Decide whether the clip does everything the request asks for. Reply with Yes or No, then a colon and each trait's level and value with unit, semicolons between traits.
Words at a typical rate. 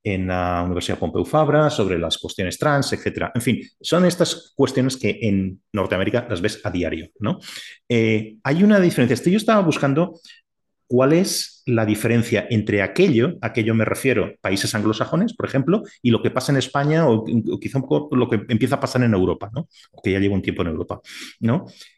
No: fast, 200 wpm